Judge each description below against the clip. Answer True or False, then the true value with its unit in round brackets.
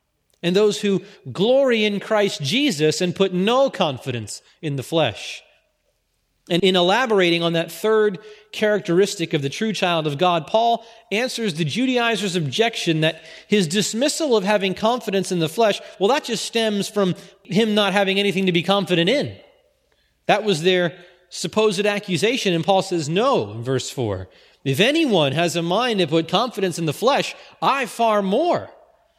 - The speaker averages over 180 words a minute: False (165 wpm)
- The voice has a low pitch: False (195 Hz)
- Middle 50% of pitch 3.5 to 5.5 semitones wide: True (4.1 semitones)